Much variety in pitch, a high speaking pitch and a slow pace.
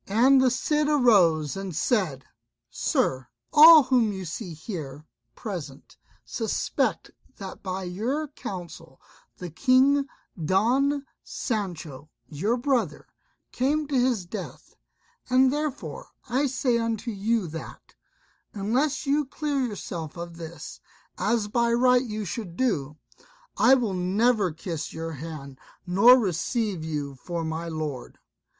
Yes: wide, 7.6 semitones; high, 205 Hz; slow, 125 wpm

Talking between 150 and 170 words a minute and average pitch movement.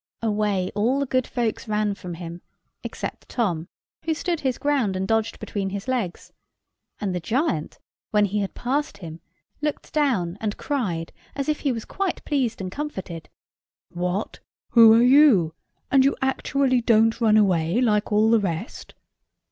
No: average, 165 wpm; wide, 5.7 semitones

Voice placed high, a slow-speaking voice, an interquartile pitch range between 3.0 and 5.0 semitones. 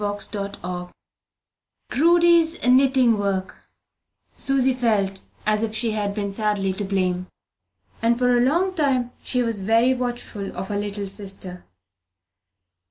Yes: high, 215 Hz; slow, 125 wpm; average, 4.1 semitones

